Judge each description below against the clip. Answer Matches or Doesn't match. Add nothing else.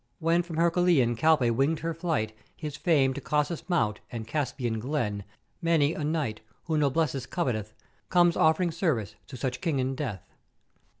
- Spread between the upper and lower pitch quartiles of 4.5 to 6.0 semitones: Matches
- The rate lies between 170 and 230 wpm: Doesn't match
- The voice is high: Doesn't match